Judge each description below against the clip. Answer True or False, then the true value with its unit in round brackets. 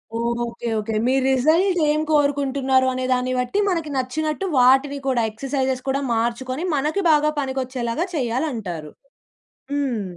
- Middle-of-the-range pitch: False (260 Hz)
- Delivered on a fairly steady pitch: False (3.3 semitones)